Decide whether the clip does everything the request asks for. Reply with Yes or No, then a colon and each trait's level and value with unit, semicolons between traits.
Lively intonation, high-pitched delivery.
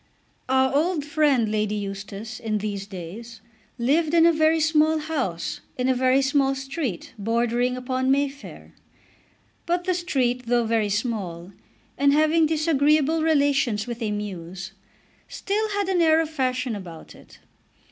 Yes: wide, 6.1 semitones; very high, 260 Hz